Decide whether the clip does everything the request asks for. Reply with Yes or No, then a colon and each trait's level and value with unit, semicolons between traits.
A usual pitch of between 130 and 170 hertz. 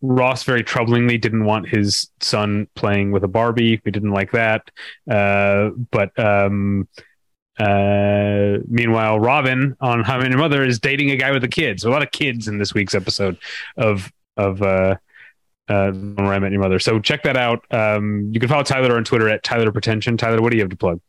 No: low, 110 Hz